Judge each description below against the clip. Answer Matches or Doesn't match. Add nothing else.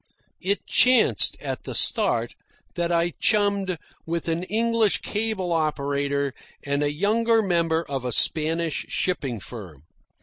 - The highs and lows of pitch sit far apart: Matches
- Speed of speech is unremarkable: Doesn't match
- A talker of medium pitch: Matches